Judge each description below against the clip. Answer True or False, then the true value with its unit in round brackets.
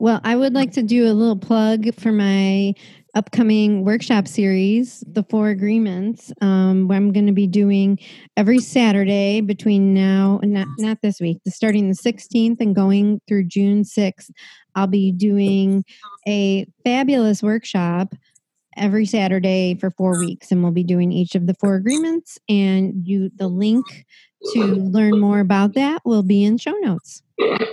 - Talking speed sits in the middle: True (160 wpm)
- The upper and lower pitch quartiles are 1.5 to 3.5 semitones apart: True (2.4 semitones)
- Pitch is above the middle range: True (205 Hz)